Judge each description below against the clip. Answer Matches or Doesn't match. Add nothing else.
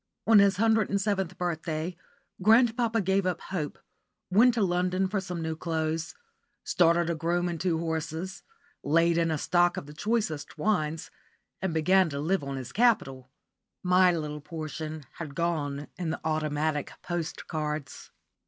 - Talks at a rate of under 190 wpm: Matches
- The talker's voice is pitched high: Doesn't match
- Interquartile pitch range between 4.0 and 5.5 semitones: Doesn't match